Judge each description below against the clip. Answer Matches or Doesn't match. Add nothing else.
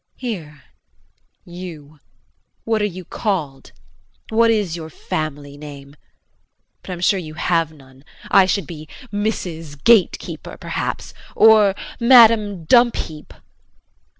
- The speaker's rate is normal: Doesn't match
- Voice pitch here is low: Doesn't match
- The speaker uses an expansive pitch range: Matches